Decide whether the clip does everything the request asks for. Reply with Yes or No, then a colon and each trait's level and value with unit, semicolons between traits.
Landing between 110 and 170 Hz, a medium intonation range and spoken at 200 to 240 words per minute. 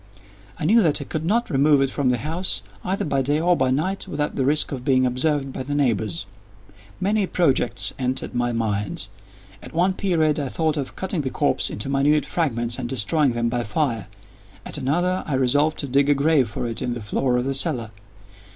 Yes: medium, 140 Hz; average, 4.2 semitones; fast, 205 wpm